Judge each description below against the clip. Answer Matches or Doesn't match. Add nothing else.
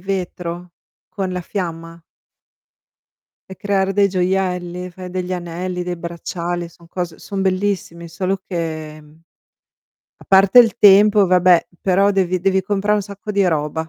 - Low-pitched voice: Doesn't match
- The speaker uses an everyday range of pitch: Doesn't match